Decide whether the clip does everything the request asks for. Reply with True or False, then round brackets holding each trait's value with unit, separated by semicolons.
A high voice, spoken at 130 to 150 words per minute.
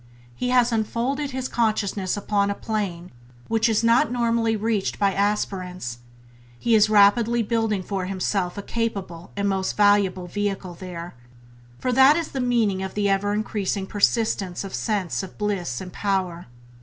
False (205 Hz; 160 wpm)